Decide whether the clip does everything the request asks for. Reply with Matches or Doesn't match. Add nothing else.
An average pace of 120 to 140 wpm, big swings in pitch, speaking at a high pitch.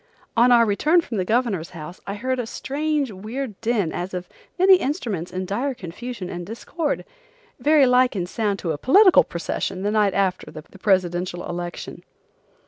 Doesn't match